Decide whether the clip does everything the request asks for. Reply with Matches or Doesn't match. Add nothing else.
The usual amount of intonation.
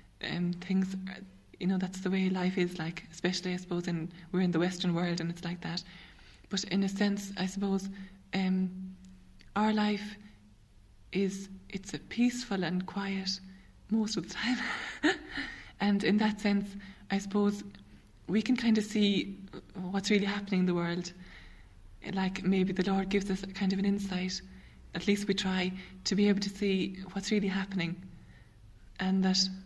Doesn't match